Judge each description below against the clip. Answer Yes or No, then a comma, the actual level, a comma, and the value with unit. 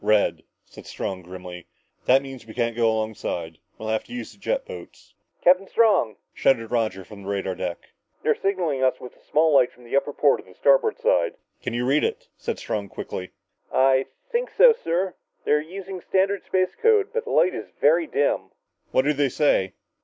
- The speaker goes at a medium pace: Yes, average, 195 wpm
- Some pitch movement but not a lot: No, wide, 8.9 semitones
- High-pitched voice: No, low, 135 Hz